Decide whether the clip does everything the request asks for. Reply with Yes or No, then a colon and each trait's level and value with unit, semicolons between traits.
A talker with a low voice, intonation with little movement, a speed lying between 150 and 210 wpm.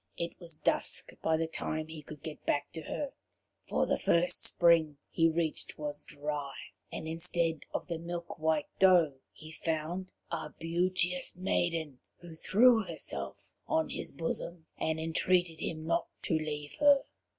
No: medium, 165 Hz; narrow, 1.9 semitones; average, 155 wpm